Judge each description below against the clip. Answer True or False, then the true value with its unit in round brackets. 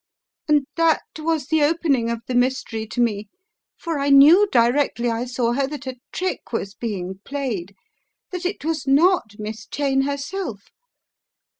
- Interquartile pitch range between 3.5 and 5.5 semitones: True (4.7 semitones)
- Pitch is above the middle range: True (270 Hz)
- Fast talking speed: False (155 wpm)